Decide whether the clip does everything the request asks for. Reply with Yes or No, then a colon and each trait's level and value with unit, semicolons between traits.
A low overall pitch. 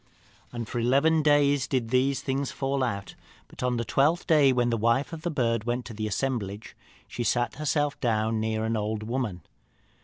Yes: low, 125 Hz